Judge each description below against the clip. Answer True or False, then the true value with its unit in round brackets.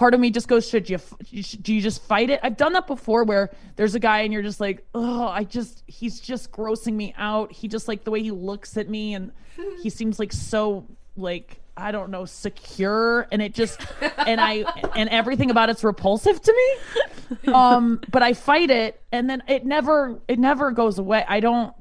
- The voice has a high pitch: True (225 Hz)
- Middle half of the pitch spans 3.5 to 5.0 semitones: False (2.8 semitones)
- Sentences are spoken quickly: True (215 wpm)